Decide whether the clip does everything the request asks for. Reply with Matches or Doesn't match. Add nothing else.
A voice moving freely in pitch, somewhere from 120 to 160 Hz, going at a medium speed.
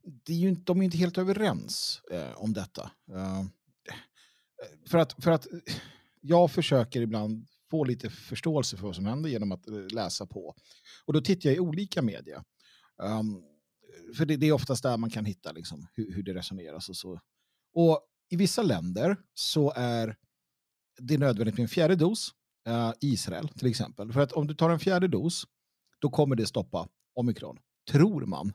Matches